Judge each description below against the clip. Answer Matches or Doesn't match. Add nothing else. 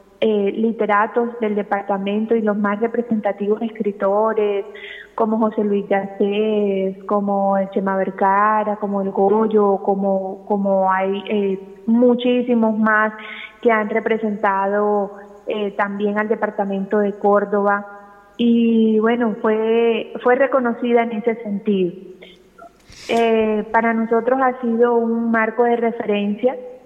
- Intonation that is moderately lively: Doesn't match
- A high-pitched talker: Matches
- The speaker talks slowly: Matches